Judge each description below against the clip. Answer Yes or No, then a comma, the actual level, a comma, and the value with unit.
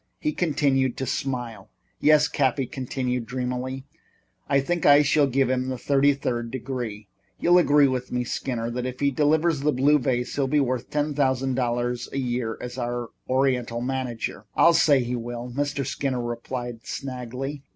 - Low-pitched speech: Yes, low, 130 Hz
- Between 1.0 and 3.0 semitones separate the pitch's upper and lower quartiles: Yes, narrow, 2.5 semitones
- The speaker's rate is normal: Yes, average, 170 wpm